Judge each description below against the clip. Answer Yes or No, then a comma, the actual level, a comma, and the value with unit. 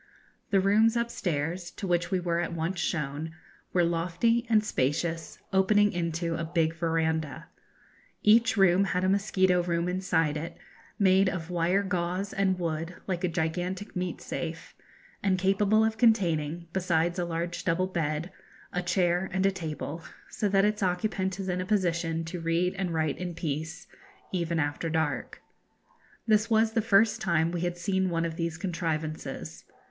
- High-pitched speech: No, medium, 175 Hz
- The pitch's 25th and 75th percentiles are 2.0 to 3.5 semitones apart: Yes, average, 2.7 semitones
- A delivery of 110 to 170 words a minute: Yes, average, 160 wpm